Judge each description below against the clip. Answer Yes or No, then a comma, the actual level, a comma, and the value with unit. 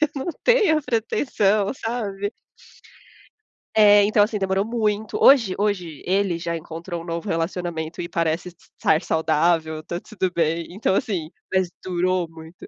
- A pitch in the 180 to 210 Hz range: Yes, medium, 185 Hz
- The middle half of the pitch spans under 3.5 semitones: No, average, 3.9 semitones